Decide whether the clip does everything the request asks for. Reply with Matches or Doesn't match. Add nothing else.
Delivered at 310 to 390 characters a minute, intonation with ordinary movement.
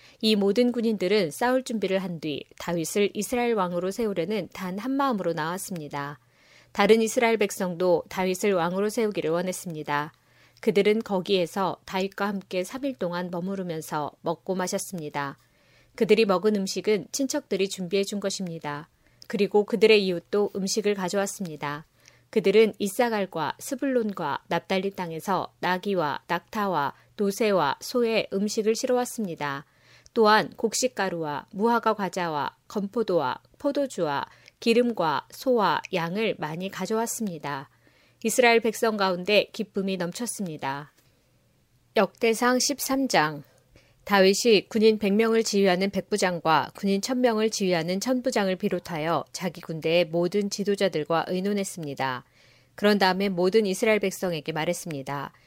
Matches